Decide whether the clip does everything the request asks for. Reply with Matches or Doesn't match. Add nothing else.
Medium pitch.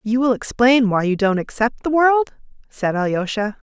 Doesn't match